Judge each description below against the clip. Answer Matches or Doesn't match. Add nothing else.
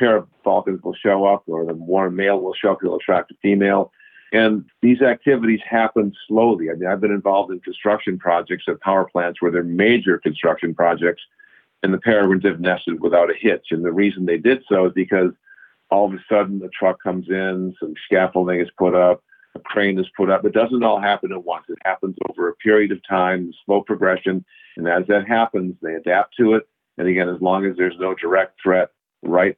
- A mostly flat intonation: Matches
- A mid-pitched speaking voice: Doesn't match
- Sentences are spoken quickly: Matches